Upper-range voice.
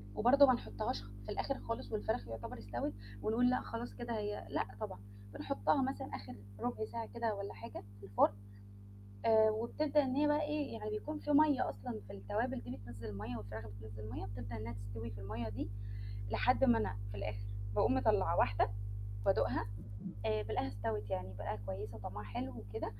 No: low, 110 Hz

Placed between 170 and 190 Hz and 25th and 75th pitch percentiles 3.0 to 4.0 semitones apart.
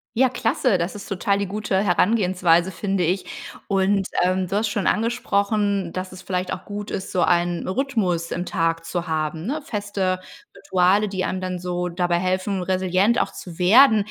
No: medium, 185 Hz; narrow, 2.4 semitones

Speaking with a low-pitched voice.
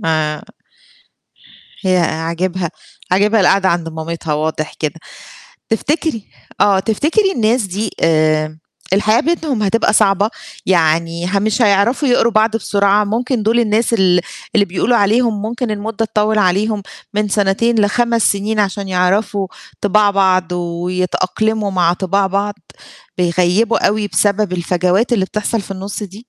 No: high, 200 Hz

